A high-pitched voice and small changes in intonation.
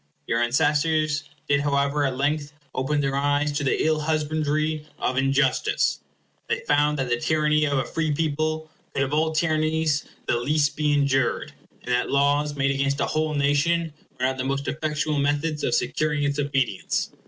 No: medium, 145 Hz; narrow, 1.7 semitones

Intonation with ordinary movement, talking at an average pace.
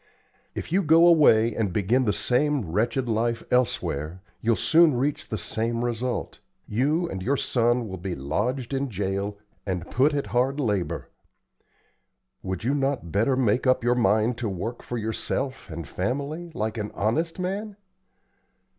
Yes: average, 4.9 semitones; average, 155 wpm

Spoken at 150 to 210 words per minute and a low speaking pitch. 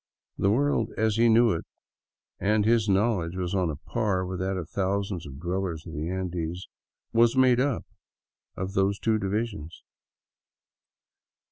Yes: average, 160 wpm; very low, 95 Hz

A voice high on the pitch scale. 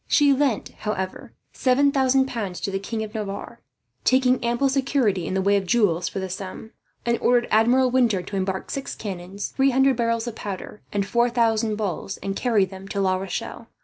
Yes: high, 220 Hz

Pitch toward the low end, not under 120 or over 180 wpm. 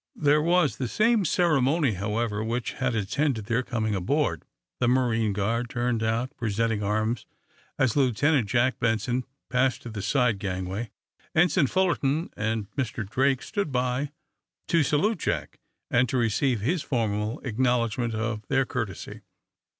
Yes: low, 120 Hz; average, 140 wpm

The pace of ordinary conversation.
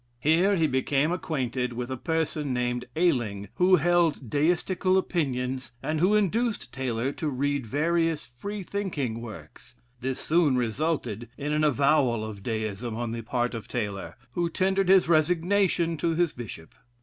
Yes: average, 150 wpm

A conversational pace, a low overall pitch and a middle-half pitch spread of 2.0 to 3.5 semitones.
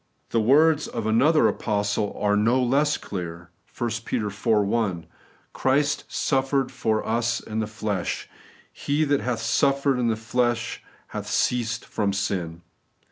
No: average, 145 wpm; low, 115 Hz; average, 4.2 semitones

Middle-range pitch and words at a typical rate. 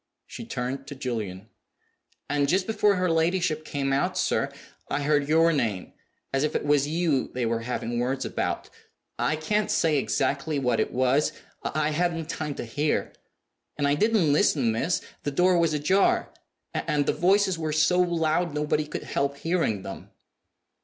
Yes: medium, 150 Hz; average, 165 wpm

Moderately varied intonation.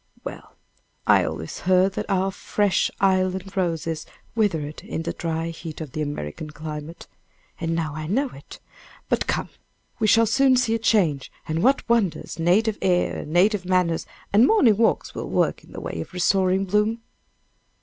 Yes: average, 4.5 semitones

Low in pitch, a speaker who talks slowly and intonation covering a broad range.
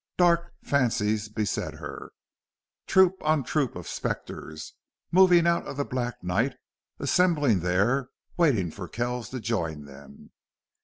Yes: low, 120 Hz; slow, 125 wpm; wide, 8.2 semitones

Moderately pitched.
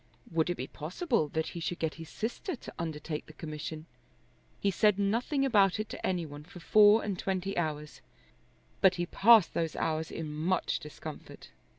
Yes: medium, 175 Hz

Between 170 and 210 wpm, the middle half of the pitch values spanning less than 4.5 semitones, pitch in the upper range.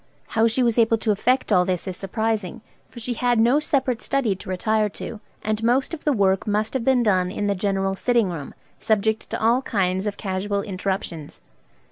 Yes: average, 200 wpm; average, 3.5 semitones; high, 215 Hz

